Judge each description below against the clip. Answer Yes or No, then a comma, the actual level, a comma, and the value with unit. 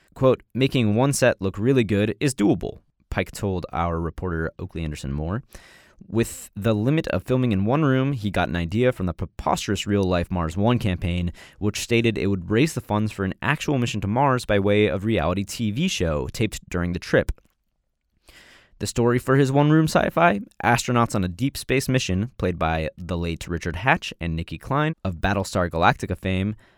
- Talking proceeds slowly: No, average, 190 wpm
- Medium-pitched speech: No, low, 105 Hz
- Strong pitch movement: Yes, wide, 5.8 semitones